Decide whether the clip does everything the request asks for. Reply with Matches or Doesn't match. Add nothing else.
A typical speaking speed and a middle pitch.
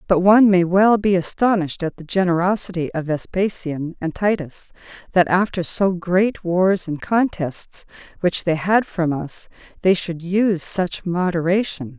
Matches